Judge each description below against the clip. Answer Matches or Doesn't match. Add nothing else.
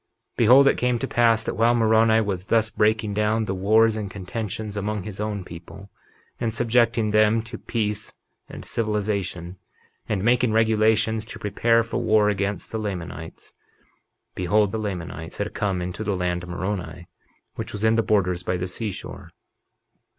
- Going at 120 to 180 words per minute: Matches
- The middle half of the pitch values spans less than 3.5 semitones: Matches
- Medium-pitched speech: Doesn't match